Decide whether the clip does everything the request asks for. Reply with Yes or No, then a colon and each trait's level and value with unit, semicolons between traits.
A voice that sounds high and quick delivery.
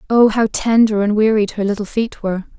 Yes: high, 215 Hz; fast, 210 wpm